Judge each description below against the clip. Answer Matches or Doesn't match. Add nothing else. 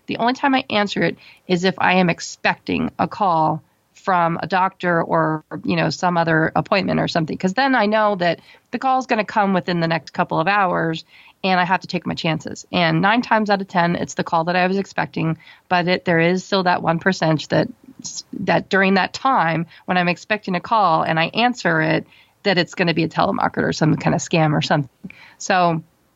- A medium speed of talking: Doesn't match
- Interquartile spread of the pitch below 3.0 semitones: Doesn't match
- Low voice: Doesn't match